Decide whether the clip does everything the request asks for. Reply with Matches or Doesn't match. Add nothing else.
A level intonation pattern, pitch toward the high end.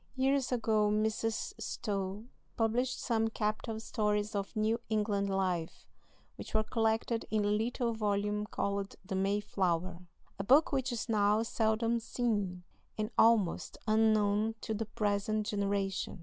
Matches